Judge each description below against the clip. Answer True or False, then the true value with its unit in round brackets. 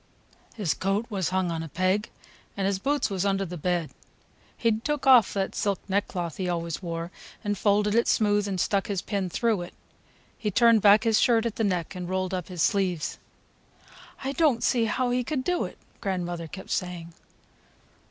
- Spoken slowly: False (190 wpm)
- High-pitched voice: True (195 Hz)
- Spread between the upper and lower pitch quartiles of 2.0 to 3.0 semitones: False (3.7 semitones)